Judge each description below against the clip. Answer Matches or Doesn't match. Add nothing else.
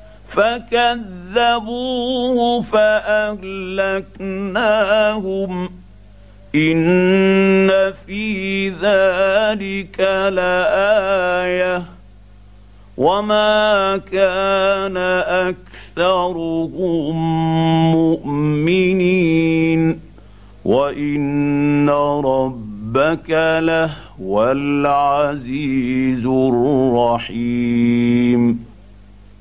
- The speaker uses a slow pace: Matches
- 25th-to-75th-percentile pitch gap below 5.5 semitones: Doesn't match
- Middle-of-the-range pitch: Matches